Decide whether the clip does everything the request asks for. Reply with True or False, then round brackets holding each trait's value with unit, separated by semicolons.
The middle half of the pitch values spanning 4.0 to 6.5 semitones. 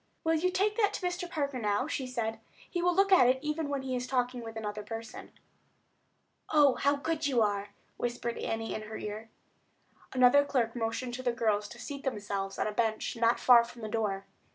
True (4.4 semitones)